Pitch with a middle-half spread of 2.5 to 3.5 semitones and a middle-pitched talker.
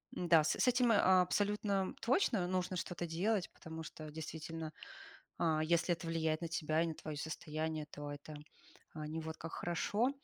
Yes: average, 2.8 semitones; medium, 165 Hz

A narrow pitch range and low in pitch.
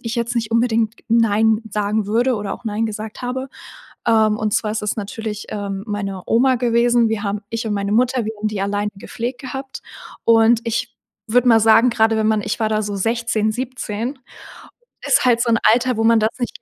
No: narrow, 2.0 semitones; high, 225 Hz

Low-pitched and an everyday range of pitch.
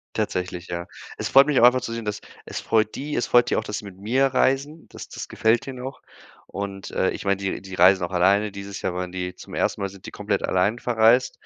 Yes: low, 105 Hz; average, 4.5 semitones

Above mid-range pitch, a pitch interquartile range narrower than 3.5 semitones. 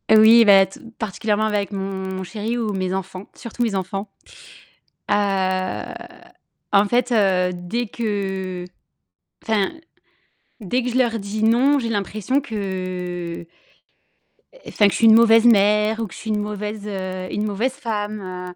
Yes: high, 205 Hz; average, 2.8 semitones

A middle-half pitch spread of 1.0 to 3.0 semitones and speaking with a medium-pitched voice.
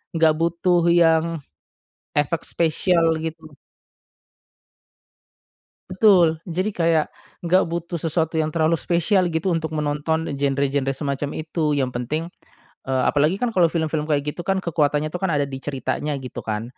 Yes: narrow, 2.6 semitones; medium, 160 Hz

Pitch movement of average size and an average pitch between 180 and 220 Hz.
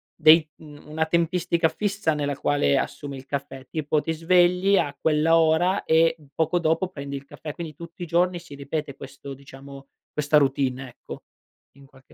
No: average, 3.2 semitones; medium, 155 Hz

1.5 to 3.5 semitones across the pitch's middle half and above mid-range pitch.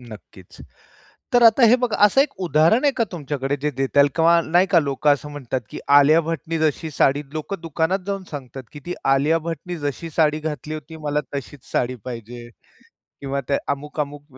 No: average, 3.2 semitones; medium, 150 Hz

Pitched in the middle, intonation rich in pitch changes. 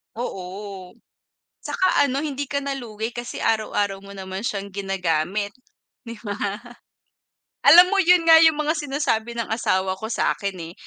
No: high, 220 Hz; wide, 6.3 semitones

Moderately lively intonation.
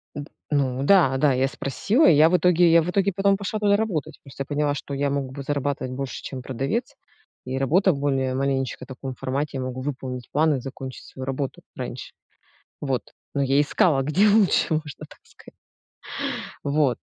Yes: average, 3.7 semitones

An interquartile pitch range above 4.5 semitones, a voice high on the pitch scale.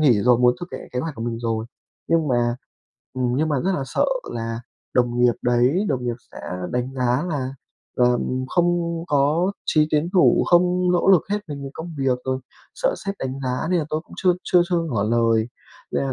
No: wide, 5.4 semitones; low, 135 Hz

